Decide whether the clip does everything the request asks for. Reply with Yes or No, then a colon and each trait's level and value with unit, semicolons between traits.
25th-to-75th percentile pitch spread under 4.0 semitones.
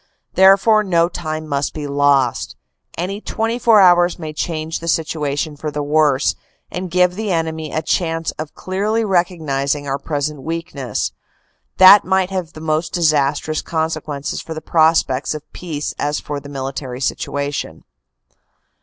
Yes: average, 3.5 semitones